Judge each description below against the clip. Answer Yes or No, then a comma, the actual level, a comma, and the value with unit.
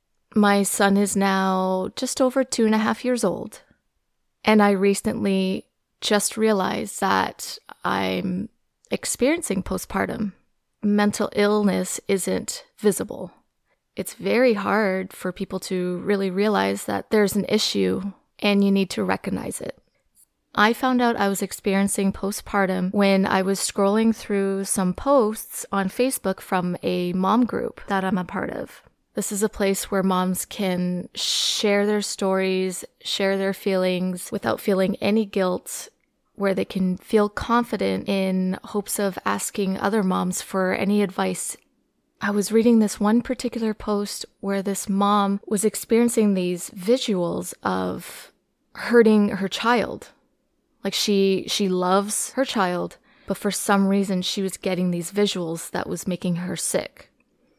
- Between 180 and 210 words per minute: No, average, 145 wpm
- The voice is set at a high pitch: Yes, high, 200 Hz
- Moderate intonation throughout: No, narrow, 2.1 semitones